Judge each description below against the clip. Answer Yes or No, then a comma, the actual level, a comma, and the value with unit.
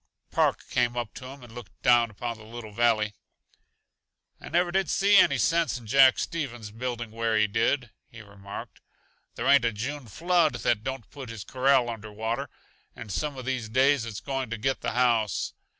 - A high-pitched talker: No, low, 120 Hz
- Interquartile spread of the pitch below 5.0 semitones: Yes, average, 3.3 semitones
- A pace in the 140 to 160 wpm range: No, average, 190 wpm